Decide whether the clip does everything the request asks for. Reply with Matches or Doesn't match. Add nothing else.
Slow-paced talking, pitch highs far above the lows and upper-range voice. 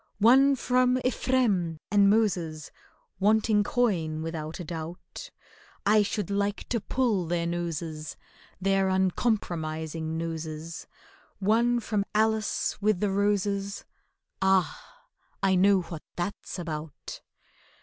Doesn't match